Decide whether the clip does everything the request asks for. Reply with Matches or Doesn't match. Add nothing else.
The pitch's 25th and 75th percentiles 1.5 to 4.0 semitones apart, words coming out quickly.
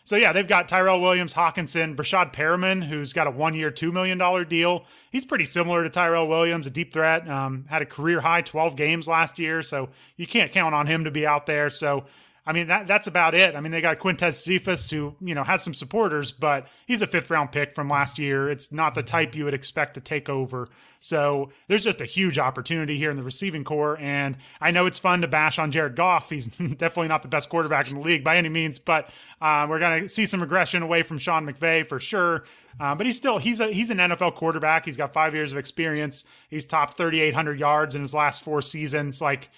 Matches